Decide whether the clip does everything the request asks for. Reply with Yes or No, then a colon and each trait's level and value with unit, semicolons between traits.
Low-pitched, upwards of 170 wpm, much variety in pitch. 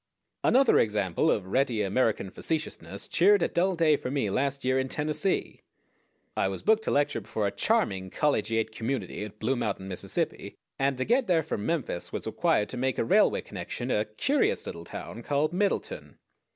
Yes: low, 130 Hz; average, 180 wpm; wide, 7.2 semitones